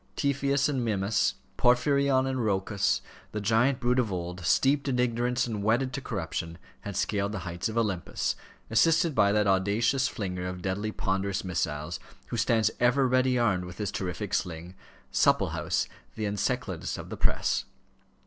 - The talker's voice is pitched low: Yes, low, 110 Hz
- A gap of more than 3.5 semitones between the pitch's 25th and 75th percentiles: Yes, average, 4.7 semitones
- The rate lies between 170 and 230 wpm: No, average, 160 wpm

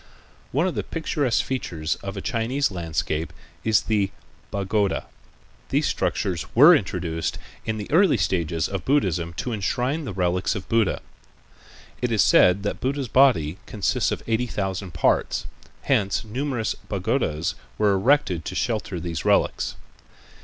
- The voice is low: Yes, low, 100 Hz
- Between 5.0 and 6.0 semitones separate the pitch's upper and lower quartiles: Yes, wide, 5.5 semitones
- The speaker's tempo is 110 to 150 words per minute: Yes, average, 140 wpm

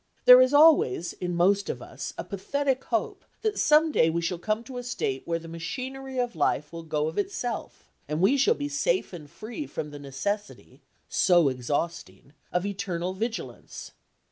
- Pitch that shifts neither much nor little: No, wide, 7.8 semitones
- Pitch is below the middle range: No, high, 195 Hz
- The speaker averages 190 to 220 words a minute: No, average, 170 wpm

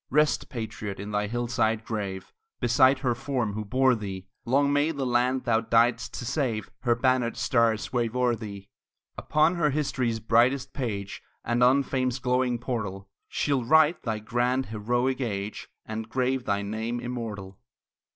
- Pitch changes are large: No, average, 3.0 semitones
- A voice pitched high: No, low, 120 Hz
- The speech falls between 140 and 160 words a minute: Yes, average, 155 wpm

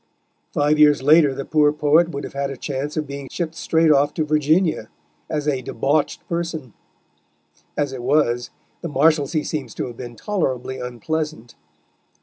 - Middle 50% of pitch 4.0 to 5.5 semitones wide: No, average, 2.8 semitones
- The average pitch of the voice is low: No, medium, 145 Hz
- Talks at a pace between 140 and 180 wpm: Yes, average, 160 wpm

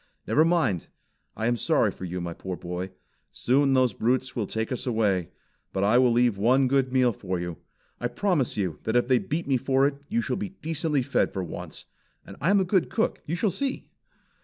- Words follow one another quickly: Yes, fast, 215 wpm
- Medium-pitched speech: No, low, 125 Hz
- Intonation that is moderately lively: No, wide, 6.3 semitones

